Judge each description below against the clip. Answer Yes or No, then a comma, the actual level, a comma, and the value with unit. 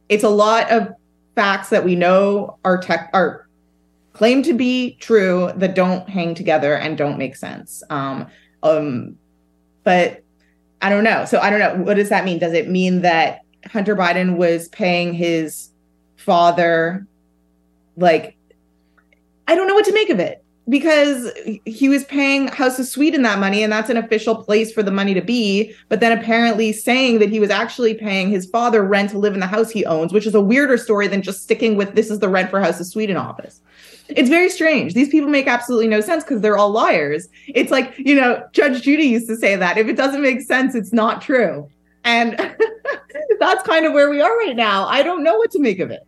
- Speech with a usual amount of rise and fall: No, wide, 6.3 semitones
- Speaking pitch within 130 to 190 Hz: No, high, 210 Hz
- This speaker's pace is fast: Yes, fast, 210 wpm